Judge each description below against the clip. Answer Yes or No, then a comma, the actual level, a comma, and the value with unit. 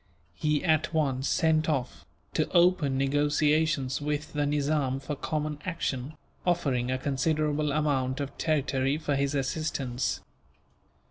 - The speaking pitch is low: No, medium, 145 Hz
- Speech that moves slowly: Yes, slow, 125 wpm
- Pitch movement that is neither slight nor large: No, narrow, 2.3 semitones